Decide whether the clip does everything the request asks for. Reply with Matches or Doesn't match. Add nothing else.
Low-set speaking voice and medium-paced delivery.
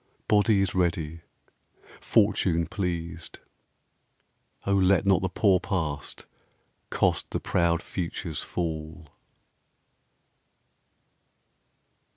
Doesn't match